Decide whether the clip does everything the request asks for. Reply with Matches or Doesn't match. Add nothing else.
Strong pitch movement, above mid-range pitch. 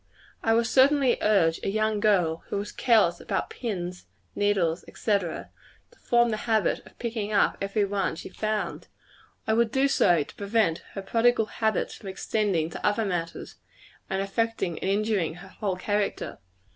Doesn't match